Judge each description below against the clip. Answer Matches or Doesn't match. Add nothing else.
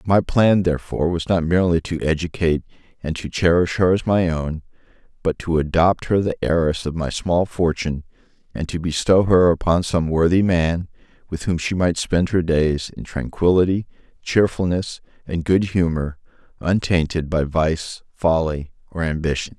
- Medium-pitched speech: Doesn't match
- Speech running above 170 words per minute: Doesn't match